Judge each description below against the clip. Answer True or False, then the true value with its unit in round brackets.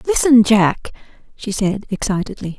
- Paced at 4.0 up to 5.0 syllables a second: True (4.6 syllables/s)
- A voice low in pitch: False (210 Hz)